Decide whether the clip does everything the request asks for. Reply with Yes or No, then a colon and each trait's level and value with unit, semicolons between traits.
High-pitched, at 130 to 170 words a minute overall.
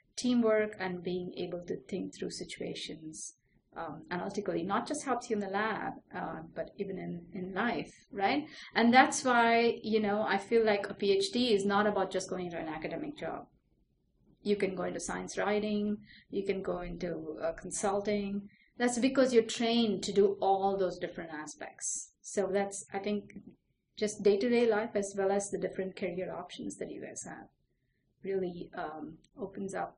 No: high, 200 Hz; average, 180 wpm